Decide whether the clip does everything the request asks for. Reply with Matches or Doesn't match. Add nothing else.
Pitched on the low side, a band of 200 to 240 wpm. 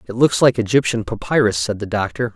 Matches